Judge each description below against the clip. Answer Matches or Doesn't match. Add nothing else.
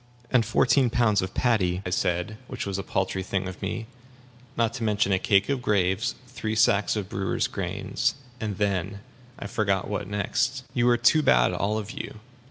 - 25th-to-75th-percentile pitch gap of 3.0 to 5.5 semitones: Matches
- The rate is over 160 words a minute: Matches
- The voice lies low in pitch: Matches